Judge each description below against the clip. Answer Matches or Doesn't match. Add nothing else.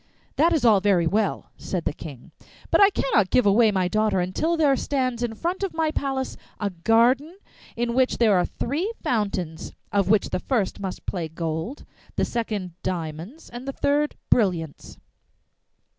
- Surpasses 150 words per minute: Matches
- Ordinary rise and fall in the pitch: Doesn't match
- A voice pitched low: Doesn't match